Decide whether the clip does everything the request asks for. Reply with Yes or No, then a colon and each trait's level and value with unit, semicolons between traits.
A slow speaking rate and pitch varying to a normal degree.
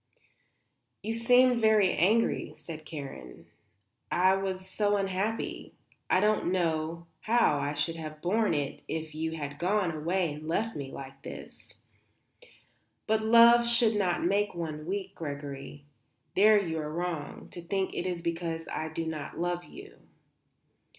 No: average, 145 wpm; average, 4.9 semitones